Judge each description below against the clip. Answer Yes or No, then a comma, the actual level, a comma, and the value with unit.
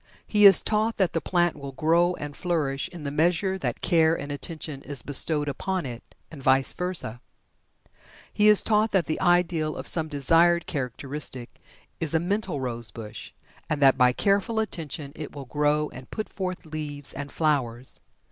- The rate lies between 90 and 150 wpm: No, average, 170 wpm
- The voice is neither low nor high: Yes, medium, 155 Hz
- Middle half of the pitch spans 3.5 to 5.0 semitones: Yes, average, 4.1 semitones